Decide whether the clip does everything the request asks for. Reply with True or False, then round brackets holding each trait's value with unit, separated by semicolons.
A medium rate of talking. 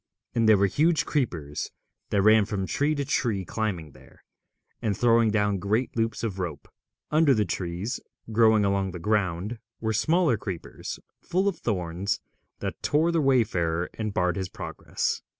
True (160 wpm)